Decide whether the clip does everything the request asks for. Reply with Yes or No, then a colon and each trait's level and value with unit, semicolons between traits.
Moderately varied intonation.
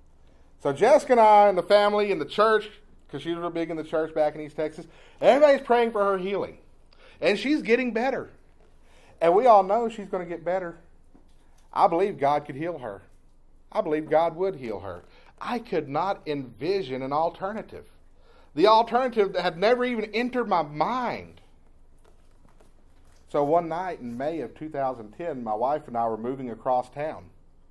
No: wide, 8.1 semitones